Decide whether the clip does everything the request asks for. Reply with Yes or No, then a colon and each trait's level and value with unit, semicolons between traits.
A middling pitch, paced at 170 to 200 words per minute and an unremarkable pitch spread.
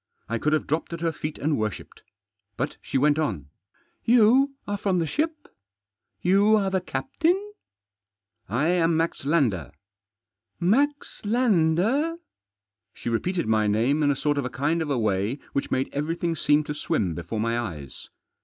No: medium, 150 Hz; average, 180 wpm; wide, 8.5 semitones